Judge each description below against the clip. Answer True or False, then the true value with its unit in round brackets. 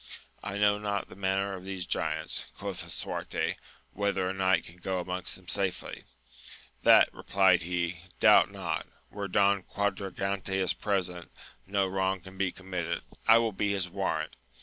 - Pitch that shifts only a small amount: True (1.5 semitones)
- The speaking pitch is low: True (95 Hz)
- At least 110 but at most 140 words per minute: False (155 wpm)